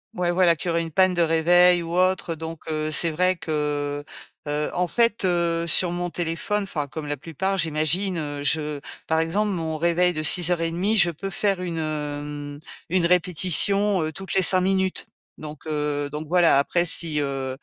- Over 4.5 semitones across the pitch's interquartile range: No, average, 2.9 semitones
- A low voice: No, medium, 165 Hz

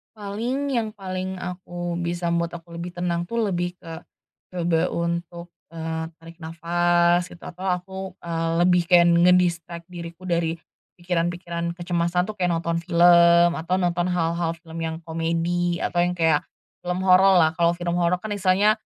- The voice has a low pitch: No, medium, 175 Hz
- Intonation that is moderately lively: No, narrow, 1.1 semitones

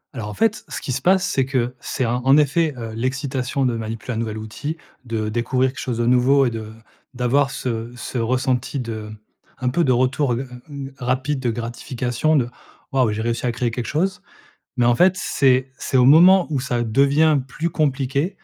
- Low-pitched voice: Yes, low, 130 Hz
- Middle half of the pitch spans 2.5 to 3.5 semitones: Yes, average, 2.9 semitones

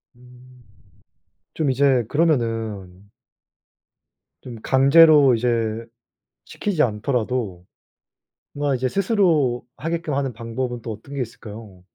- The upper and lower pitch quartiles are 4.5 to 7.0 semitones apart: No, average, 3.9 semitones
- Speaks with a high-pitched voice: No, low, 125 Hz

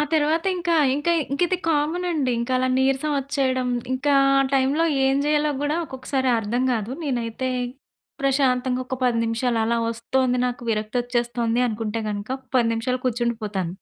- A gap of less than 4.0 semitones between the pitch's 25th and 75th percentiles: Yes, average, 3.3 semitones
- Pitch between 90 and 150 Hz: No, very high, 255 Hz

